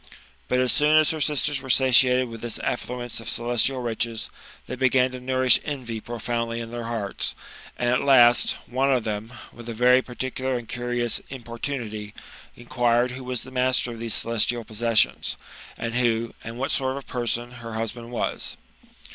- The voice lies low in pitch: Yes, low, 120 Hz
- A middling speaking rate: Yes, average, 180 wpm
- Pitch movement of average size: No, narrow, 1.7 semitones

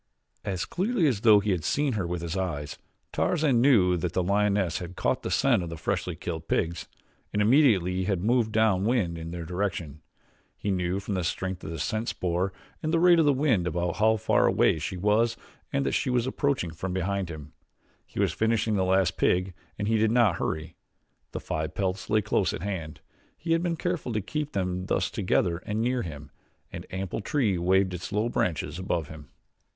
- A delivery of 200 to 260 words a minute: Yes, fast, 205 wpm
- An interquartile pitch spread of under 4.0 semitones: No, average, 4.5 semitones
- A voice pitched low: Yes, very low, 95 Hz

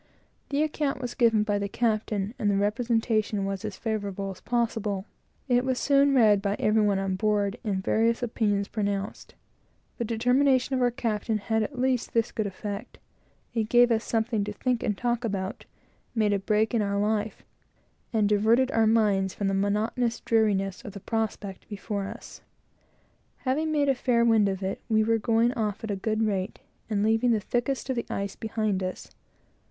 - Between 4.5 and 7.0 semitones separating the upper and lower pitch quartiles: No, average, 2.8 semitones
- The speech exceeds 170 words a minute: Yes, average, 185 wpm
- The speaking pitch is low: No, high, 220 Hz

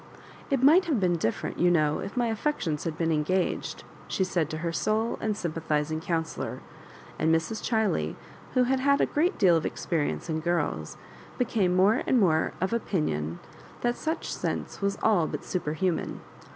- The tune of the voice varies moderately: No, wide, 6.0 semitones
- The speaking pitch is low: No, medium, 180 Hz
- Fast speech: No, average, 170 wpm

